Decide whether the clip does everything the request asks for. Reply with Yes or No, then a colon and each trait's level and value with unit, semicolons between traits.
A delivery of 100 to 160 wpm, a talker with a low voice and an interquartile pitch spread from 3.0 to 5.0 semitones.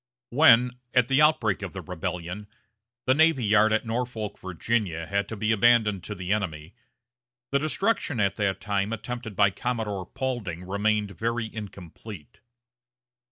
Yes: average, 145 wpm; low, 105 Hz; average, 3.6 semitones